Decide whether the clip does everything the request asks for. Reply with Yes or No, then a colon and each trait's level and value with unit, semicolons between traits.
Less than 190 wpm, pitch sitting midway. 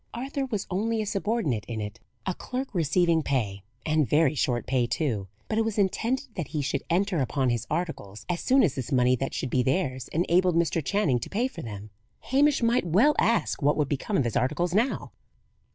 No: fast, 205 wpm; medium, 165 Hz